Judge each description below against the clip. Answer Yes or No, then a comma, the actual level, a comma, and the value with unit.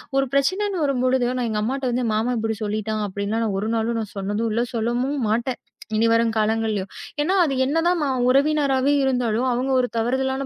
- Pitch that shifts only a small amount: No, average, 3.4 semitones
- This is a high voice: Yes, high, 240 Hz